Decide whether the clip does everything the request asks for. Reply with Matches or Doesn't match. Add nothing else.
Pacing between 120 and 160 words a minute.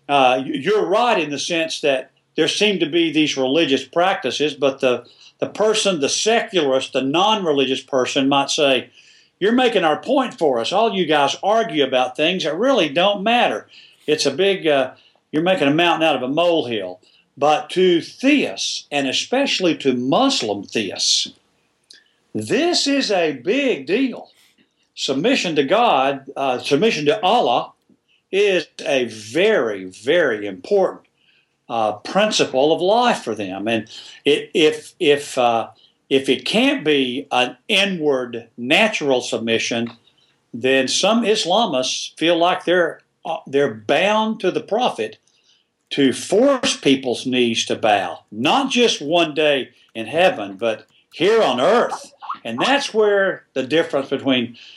Matches